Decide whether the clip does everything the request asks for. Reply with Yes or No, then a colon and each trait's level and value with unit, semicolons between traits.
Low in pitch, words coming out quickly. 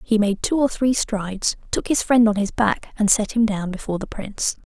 No: high, 215 Hz; fast, 245 wpm